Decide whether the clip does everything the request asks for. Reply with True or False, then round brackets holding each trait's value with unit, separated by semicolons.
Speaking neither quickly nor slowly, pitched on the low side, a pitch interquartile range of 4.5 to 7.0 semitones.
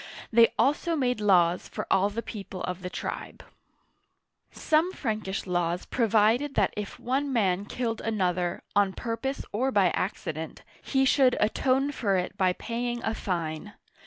False (155 wpm; 215 Hz; 5.2 semitones)